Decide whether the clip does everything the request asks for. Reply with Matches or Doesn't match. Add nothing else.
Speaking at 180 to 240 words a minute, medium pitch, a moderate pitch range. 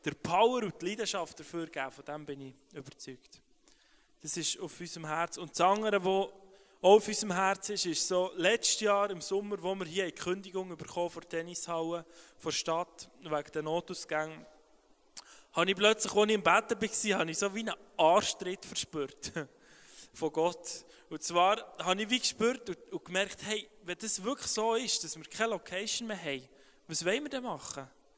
Matches